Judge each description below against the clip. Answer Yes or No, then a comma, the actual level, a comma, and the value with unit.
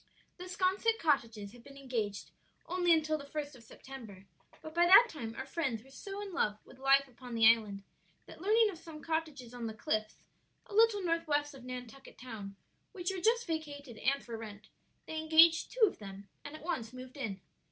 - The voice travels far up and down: Yes, wide, 6.4 semitones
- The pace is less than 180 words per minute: No, average, 200 wpm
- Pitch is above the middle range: Yes, very high, 275 Hz